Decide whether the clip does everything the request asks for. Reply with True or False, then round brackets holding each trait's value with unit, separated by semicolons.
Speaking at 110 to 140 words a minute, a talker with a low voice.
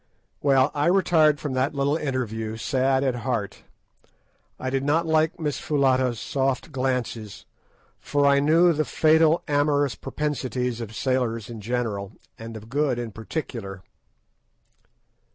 True (135 wpm; 130 Hz)